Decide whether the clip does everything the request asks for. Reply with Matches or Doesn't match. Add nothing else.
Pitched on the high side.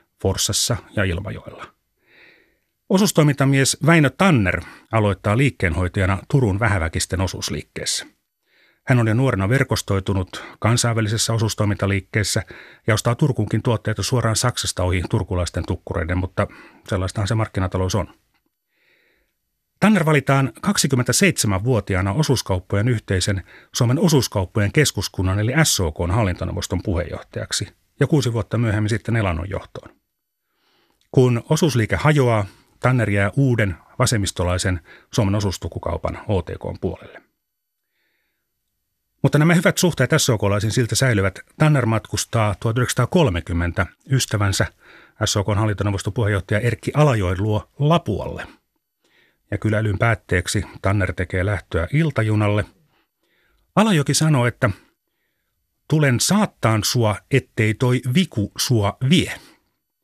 Doesn't match